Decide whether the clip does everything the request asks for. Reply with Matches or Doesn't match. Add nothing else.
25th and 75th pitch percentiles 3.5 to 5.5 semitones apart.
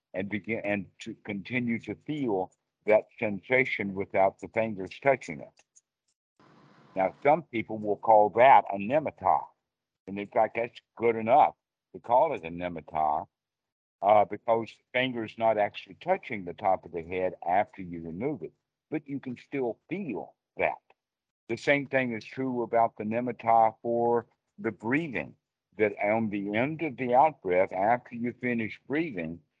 Doesn't match